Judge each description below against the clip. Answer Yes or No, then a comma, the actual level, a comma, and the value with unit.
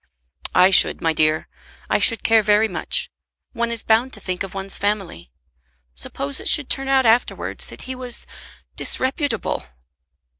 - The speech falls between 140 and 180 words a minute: Yes, average, 155 wpm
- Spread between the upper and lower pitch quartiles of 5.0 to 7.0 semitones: Yes, wide, 5.4 semitones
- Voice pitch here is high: Yes, high, 220 Hz